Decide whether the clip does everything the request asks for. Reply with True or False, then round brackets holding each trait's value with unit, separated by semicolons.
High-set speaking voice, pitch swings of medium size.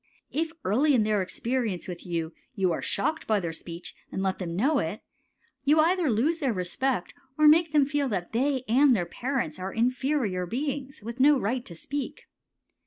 False (240 Hz; 7.2 semitones)